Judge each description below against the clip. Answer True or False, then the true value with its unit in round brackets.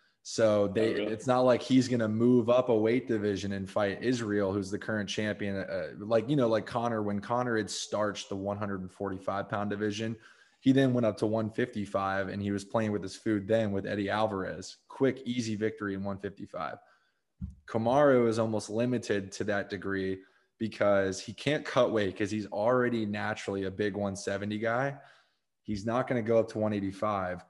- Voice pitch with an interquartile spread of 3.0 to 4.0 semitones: False (2.5 semitones)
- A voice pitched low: True (105 Hz)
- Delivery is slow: False (185 wpm)